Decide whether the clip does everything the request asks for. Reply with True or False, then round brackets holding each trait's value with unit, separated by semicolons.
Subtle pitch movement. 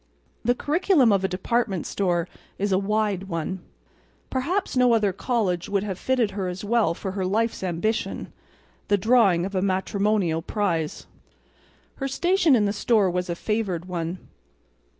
False (3.9 semitones)